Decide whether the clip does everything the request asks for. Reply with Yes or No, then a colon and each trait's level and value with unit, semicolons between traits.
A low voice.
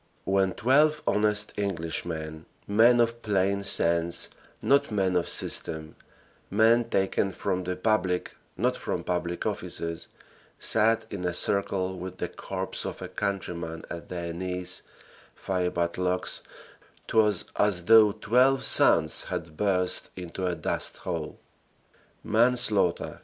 Yes: very low, 95 Hz